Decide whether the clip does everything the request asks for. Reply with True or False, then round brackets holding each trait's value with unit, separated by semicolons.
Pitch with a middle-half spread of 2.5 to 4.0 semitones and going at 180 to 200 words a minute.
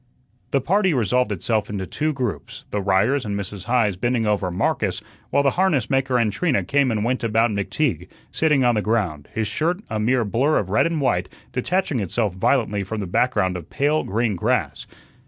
False (5.1 semitones; 190 wpm)